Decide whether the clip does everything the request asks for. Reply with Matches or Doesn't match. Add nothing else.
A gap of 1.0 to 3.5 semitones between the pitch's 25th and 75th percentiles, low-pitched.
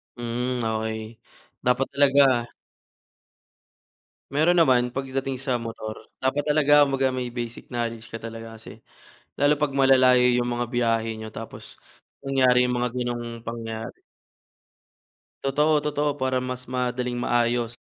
Matches